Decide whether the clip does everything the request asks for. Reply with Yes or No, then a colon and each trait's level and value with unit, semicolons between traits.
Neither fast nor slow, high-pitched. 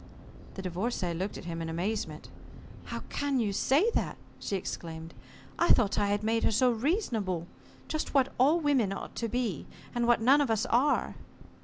Yes: average, 180 wpm; high, 225 Hz